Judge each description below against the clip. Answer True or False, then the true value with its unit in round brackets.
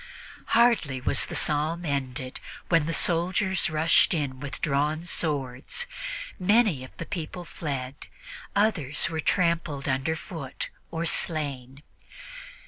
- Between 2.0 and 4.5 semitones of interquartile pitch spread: True (3.7 semitones)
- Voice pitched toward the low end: False (155 Hz)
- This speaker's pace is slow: True (115 wpm)